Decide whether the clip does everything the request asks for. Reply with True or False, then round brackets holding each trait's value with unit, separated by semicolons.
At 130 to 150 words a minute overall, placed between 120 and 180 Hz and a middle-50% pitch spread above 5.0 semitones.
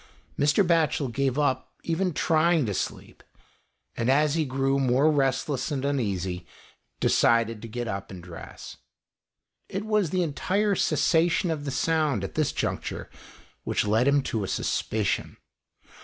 True (145 wpm; 140 Hz; 5.5 semitones)